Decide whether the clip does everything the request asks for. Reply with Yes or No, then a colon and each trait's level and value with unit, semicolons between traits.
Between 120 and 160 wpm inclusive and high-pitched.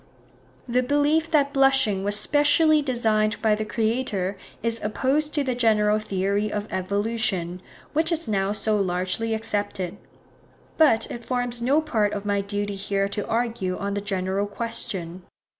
Yes: average, 150 wpm; high, 215 Hz